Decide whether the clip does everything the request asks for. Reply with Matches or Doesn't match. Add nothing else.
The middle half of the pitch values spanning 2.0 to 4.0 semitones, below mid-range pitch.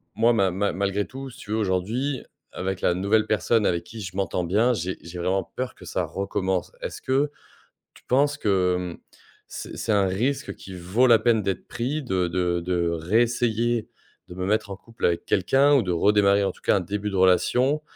Doesn't match